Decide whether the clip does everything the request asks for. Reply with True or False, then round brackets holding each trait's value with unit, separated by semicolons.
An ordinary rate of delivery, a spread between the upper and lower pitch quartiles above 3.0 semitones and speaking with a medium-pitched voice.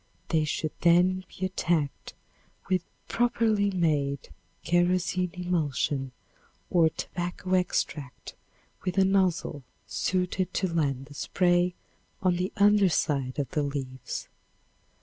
False (110 wpm; 3.8 semitones; 175 Hz)